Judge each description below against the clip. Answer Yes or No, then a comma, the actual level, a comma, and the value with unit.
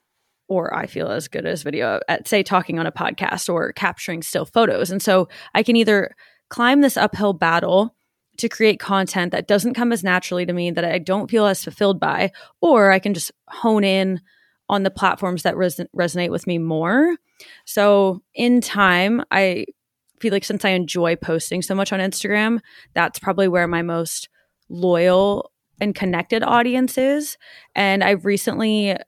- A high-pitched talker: Yes, high, 195 Hz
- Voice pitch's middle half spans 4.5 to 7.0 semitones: No, average, 3.3 semitones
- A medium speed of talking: Yes, average, 175 wpm